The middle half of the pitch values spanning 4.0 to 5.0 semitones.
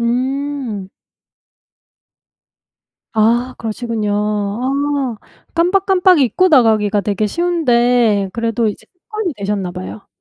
No: wide, 5.4 semitones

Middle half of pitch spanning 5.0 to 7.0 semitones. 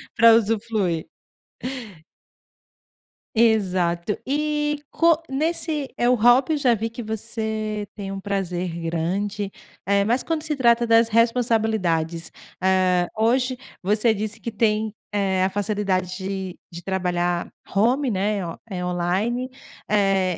No: average, 3.9 semitones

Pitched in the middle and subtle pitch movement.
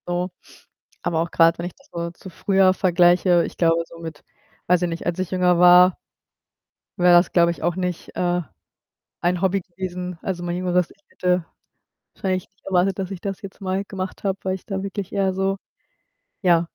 Yes: medium, 180 Hz; narrow, 1.6 semitones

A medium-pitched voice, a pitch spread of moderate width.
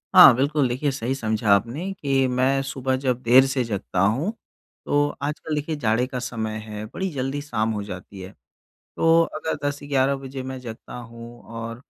No: low, 130 Hz; average, 3.7 semitones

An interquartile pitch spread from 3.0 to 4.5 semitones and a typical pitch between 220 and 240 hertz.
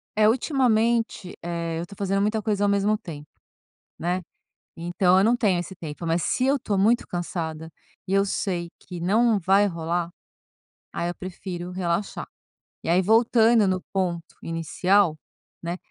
No: average, 3.5 semitones; medium, 185 Hz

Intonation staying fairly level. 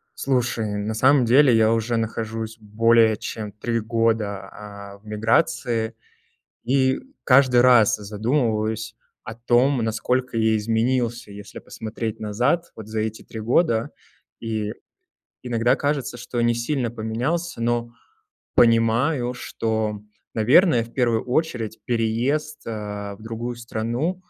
Yes: narrow, 2.0 semitones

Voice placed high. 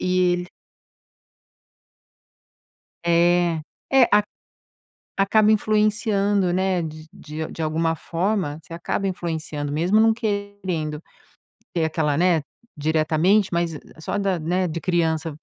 No: medium, 175 Hz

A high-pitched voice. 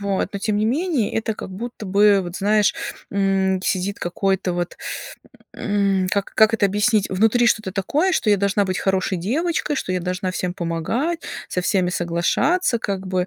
Yes: high, 200 Hz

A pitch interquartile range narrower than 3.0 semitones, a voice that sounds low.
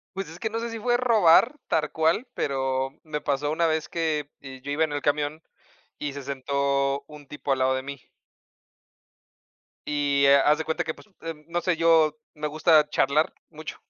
No: narrow, 2.6 semitones; medium, 150 Hz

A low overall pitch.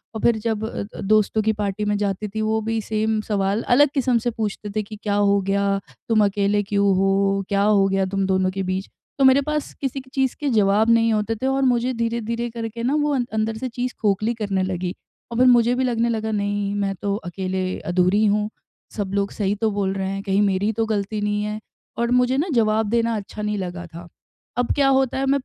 No: high, 215 Hz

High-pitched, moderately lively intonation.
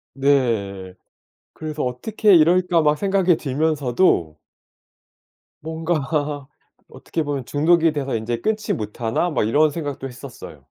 No: medium, 145 Hz; average, 4.8 semitones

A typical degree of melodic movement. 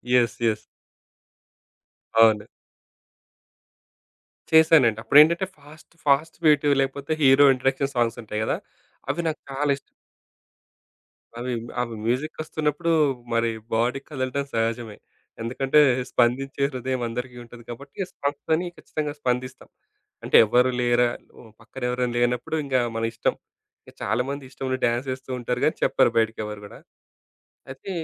Yes: average, 3.1 semitones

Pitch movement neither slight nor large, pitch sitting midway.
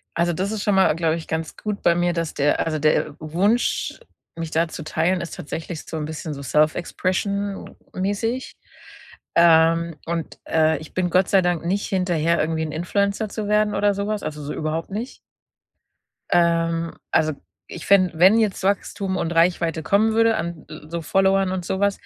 Yes: average, 3.6 semitones; medium, 175 Hz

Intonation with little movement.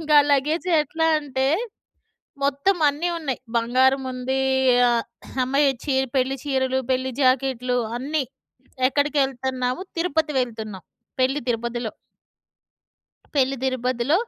Yes: narrow, 2.2 semitones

